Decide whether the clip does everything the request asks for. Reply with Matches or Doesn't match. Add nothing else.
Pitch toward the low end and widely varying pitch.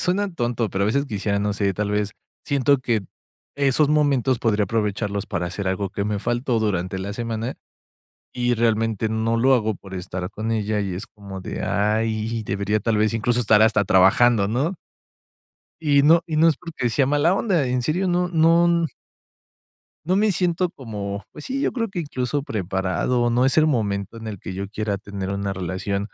Matches